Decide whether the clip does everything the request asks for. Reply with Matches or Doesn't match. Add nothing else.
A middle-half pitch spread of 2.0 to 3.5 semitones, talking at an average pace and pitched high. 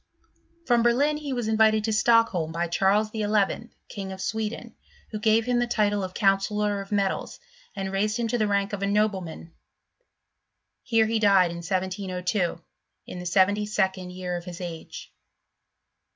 Matches